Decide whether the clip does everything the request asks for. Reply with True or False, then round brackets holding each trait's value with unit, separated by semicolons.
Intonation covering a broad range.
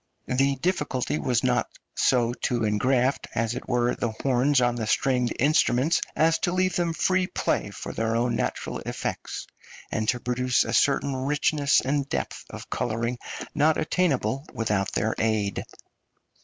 False (3.7 semitones)